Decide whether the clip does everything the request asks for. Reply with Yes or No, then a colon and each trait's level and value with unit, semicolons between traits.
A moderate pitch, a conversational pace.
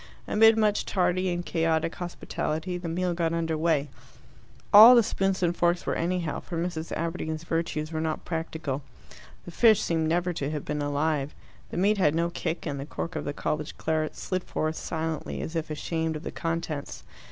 Yes: medium, 165 Hz; average, 185 wpm